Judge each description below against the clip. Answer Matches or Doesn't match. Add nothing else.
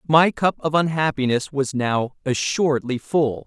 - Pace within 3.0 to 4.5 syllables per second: Matches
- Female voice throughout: Doesn't match